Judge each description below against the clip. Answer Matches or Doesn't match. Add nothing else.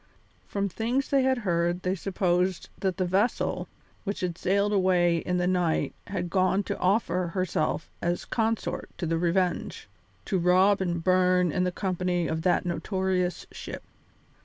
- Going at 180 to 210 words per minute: Doesn't match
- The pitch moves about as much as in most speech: Doesn't match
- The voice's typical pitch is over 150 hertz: Matches